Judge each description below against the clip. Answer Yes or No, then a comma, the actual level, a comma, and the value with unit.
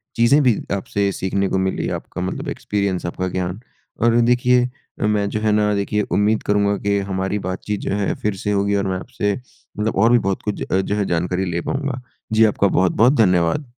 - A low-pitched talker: Yes, low, 100 Hz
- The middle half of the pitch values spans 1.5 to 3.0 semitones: Yes, narrow, 2.6 semitones